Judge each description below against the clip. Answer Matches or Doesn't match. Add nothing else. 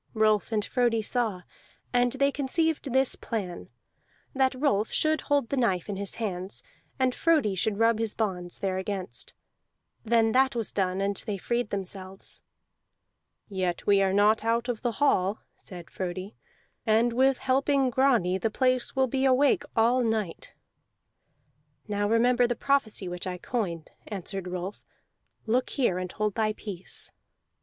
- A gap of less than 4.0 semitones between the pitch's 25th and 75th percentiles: Doesn't match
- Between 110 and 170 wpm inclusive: Matches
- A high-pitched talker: Matches